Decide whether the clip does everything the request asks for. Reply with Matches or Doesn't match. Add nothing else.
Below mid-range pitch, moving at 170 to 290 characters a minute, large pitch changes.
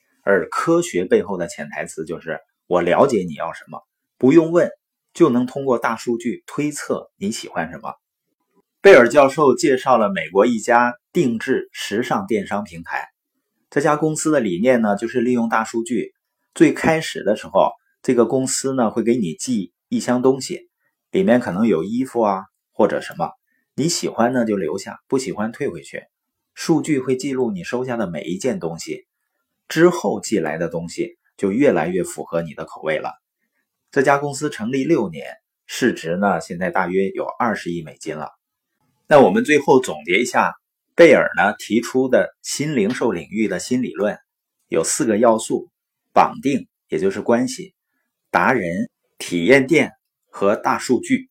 Matches